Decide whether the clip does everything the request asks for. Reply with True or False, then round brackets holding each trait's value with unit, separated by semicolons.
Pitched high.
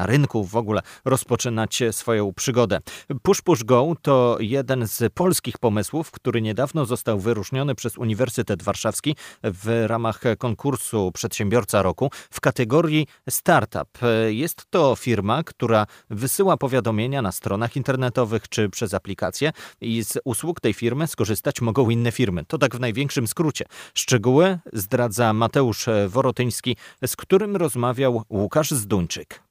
False (120 Hz)